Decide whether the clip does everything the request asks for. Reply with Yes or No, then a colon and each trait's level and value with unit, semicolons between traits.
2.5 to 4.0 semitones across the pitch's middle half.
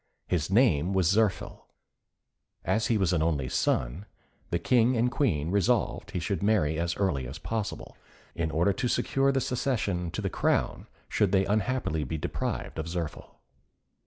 No: wide, 5.5 semitones